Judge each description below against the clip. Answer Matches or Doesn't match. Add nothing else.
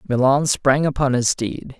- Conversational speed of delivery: Matches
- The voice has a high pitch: Doesn't match